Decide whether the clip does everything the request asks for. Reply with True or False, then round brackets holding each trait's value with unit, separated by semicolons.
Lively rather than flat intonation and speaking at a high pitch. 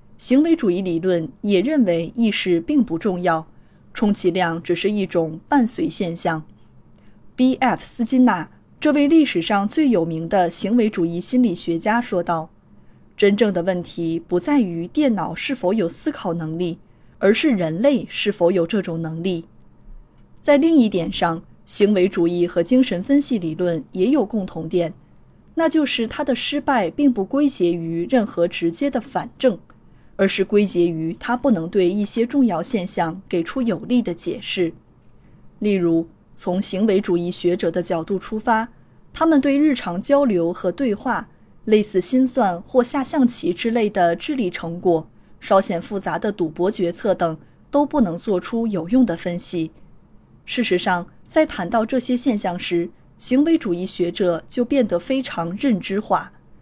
True (6.4 semitones; 195 Hz)